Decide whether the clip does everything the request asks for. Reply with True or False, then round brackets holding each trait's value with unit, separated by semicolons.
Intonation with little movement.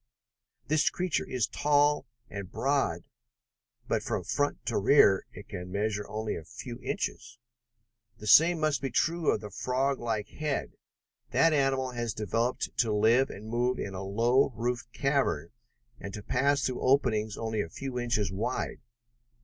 False (4.7 semitones)